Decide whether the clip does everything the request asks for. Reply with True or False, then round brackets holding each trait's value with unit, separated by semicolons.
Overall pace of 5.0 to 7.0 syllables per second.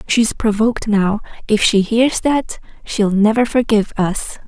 False (4.3 syllables/s)